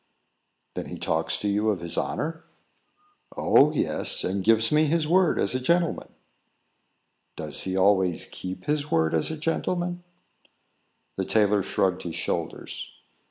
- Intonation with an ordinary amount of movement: No, wide, 9.0 semitones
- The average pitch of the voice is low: Yes, low, 110 Hz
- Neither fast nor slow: Yes, average, 145 wpm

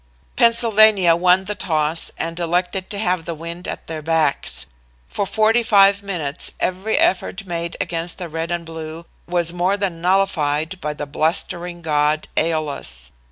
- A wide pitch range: No, average, 3.1 semitones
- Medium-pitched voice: Yes, medium, 170 Hz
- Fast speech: No, average, 155 wpm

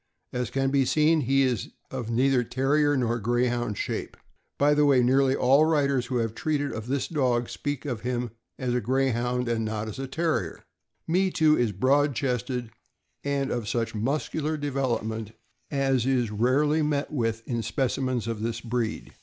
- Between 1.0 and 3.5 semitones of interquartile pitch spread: Yes, average, 3.2 semitones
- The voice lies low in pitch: Yes, low, 130 Hz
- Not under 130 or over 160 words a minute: No, average, 180 wpm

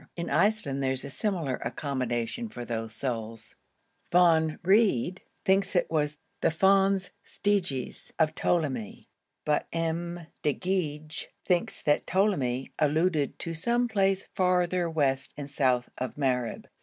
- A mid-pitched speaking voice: Yes, medium, 160 Hz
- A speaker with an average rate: No, slow, 130 wpm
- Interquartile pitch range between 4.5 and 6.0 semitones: Yes, wide, 5.6 semitones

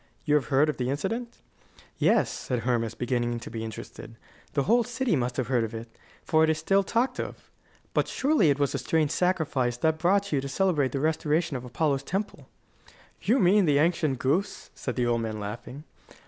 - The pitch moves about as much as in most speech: No, wide, 6.2 semitones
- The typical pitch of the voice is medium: Yes, medium, 145 Hz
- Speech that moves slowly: No, average, 200 wpm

